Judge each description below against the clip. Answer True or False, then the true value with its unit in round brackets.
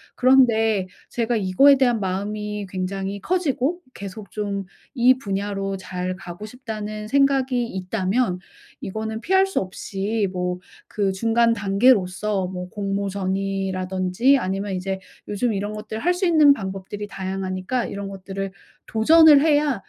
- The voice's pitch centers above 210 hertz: False (205 Hz)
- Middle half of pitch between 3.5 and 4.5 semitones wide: True (4.1 semitones)